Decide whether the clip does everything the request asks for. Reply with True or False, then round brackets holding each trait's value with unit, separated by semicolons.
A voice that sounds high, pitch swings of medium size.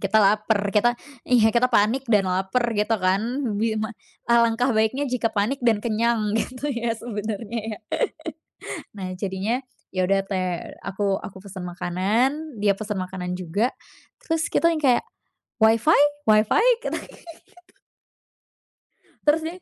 True (220 Hz; 3.6 semitones)